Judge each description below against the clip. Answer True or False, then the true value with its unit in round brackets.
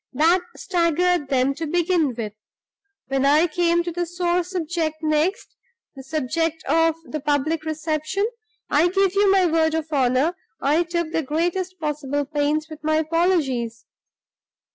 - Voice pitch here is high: True (320 Hz)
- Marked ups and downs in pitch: False (2.9 semitones)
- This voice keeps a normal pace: True (145 wpm)